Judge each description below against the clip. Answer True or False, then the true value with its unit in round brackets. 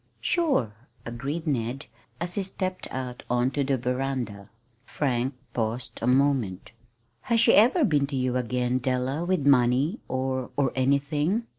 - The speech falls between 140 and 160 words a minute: True (145 wpm)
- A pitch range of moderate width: True (3.3 semitones)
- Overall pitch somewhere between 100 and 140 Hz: True (135 Hz)